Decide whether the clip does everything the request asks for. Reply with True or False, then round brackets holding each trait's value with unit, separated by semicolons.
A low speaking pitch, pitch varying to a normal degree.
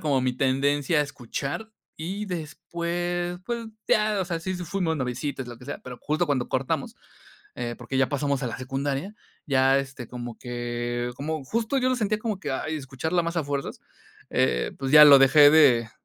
False (145 Hz; 4.9 semitones)